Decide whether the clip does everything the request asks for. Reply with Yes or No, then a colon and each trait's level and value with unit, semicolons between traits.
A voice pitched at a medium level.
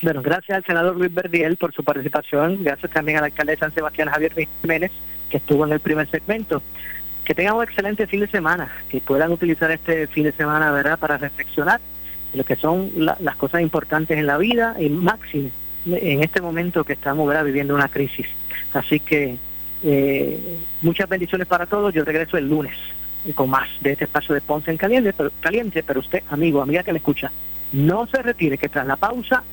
Yes: medium, 155 Hz